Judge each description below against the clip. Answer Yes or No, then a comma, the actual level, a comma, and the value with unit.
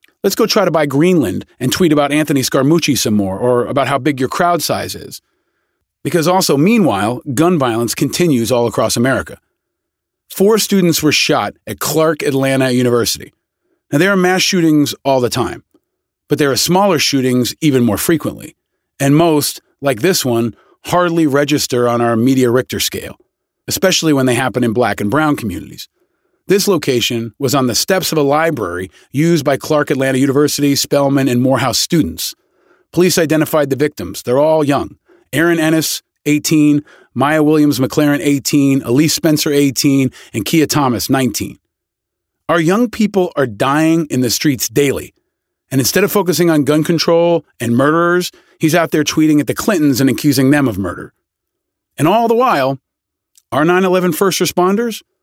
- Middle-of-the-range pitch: Yes, medium, 145 Hz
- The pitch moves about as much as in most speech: Yes, average, 4.3 semitones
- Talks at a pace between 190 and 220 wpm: No, average, 165 wpm